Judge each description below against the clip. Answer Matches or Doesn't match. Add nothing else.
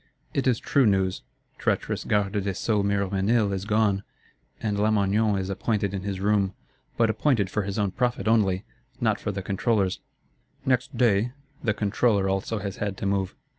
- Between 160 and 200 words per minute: Matches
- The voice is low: Matches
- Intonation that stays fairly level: Matches